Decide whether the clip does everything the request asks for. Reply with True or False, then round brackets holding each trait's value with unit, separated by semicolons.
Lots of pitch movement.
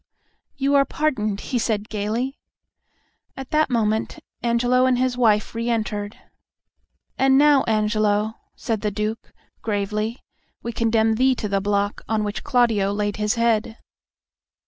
False (2.8 semitones)